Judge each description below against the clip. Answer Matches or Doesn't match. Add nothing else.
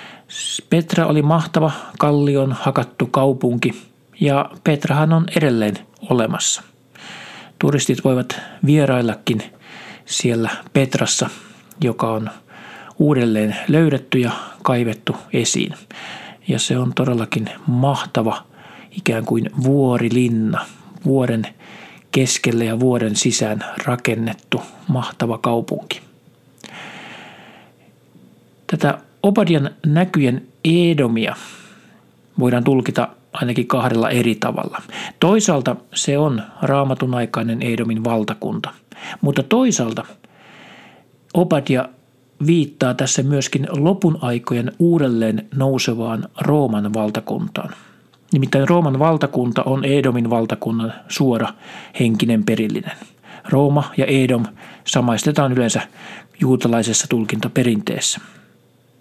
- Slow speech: Matches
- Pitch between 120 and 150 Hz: Matches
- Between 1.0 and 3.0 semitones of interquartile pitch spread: Doesn't match